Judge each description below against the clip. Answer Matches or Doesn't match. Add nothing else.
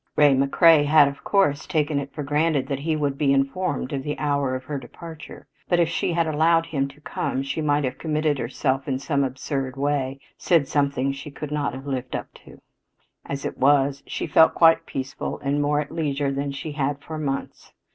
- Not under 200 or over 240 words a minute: Matches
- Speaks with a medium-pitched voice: Matches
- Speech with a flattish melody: Matches